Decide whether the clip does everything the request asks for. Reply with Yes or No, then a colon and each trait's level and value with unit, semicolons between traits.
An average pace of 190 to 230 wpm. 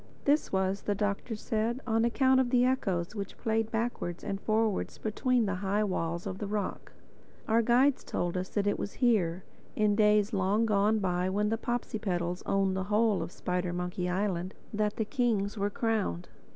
No: average, 175 wpm